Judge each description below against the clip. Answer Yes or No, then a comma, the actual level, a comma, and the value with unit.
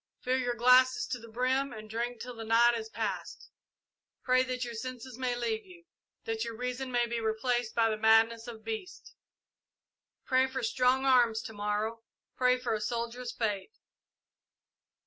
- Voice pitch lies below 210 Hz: No, high, 240 Hz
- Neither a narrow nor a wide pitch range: No, narrow, 2.2 semitones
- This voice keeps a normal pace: Yes, average, 165 wpm